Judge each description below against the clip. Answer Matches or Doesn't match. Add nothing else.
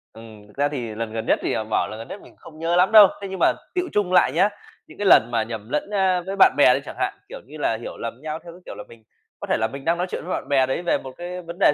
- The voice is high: Doesn't match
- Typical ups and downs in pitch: Doesn't match